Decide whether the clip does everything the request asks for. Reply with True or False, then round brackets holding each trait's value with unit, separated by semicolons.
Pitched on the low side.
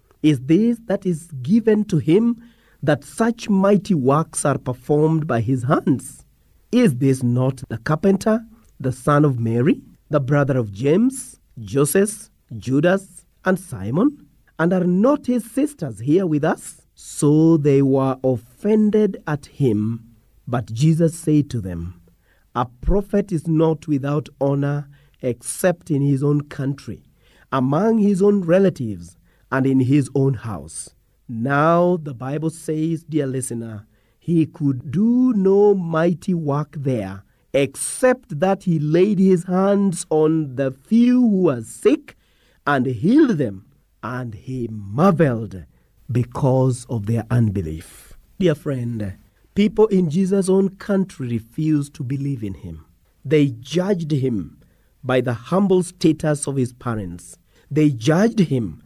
False (145 Hz)